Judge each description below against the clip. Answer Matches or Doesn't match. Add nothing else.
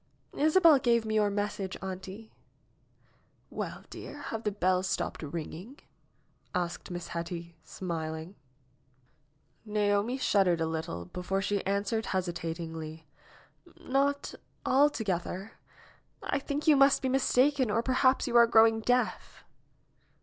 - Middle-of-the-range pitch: Doesn't match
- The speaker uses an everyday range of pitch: Doesn't match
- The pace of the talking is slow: Matches